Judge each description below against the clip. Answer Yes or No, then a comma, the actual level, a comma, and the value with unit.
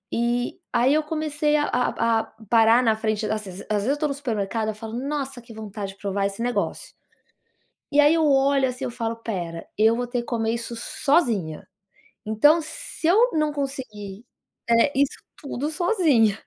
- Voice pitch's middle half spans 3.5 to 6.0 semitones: Yes, average, 4.8 semitones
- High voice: Yes, high, 240 Hz